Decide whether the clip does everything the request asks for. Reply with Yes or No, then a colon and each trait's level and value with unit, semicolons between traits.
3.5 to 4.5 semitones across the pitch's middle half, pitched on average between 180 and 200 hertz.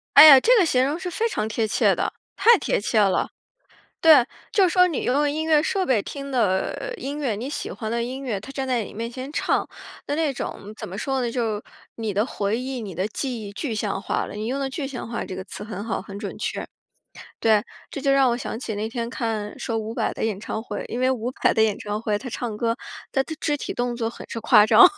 No: average, 4.2 semitones; high, 240 Hz